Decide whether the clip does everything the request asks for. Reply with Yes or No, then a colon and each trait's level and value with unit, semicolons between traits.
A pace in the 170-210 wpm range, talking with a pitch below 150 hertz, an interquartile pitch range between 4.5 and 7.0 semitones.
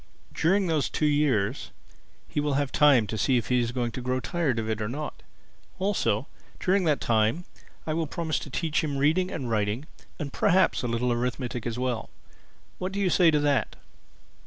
Yes: average, 195 wpm; medium, 140 Hz; average, 5.1 semitones